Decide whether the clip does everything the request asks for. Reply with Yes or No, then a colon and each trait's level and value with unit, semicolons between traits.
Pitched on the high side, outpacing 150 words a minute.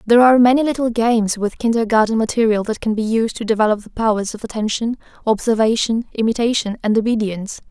Yes: high, 225 Hz; average, 170 wpm